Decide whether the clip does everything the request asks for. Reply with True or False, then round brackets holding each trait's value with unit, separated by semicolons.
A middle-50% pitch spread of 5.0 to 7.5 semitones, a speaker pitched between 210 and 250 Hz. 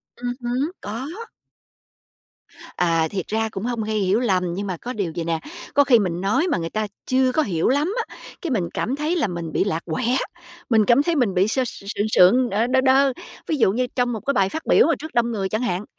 True (5.4 semitones; 225 Hz)